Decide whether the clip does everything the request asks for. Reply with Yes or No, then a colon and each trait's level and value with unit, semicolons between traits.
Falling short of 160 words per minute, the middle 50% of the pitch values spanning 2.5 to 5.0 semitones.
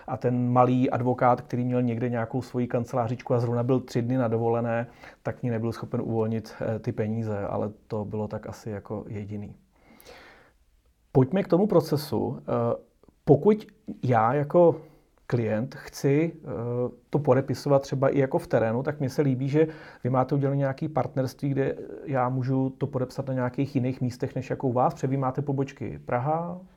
No: average, 165 wpm; average, 2.8 semitones